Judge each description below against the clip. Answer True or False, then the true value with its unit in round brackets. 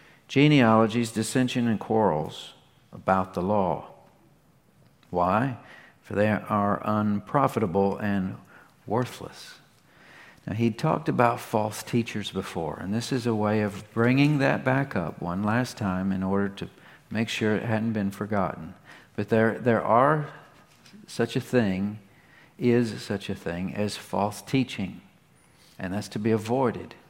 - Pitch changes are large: False (3.7 semitones)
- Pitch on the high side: False (110 Hz)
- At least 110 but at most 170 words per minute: True (135 wpm)